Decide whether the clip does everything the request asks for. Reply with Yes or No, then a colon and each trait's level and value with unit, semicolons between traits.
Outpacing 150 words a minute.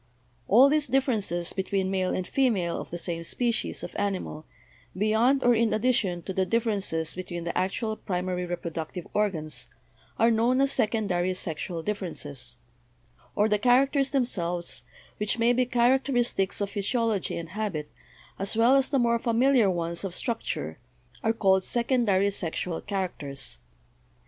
No: average, 145 wpm